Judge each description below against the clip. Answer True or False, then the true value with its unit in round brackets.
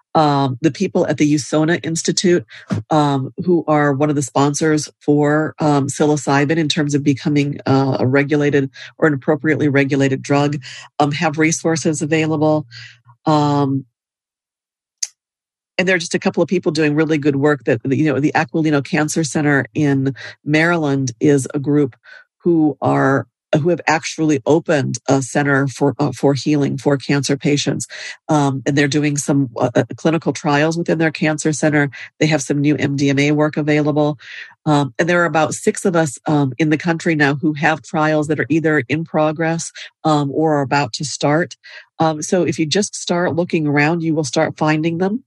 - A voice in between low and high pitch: True (150 Hz)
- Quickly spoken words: False (170 wpm)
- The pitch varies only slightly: True (2.0 semitones)